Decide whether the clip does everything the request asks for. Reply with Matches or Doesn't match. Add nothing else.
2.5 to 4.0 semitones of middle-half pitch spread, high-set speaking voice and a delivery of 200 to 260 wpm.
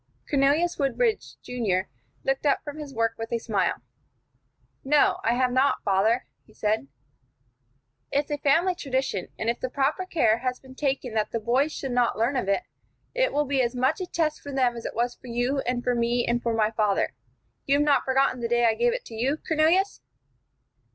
Matches